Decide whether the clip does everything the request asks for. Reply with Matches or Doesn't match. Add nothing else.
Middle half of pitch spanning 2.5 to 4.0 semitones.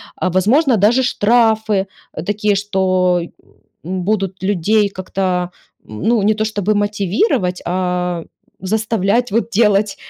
Matches